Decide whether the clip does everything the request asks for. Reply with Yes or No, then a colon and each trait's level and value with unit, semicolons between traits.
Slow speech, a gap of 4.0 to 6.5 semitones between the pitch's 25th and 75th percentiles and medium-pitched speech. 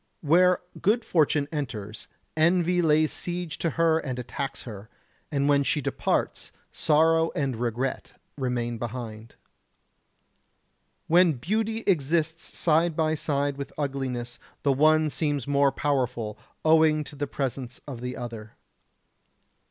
Yes: slow, 125 wpm; average, 4.3 semitones; medium, 145 Hz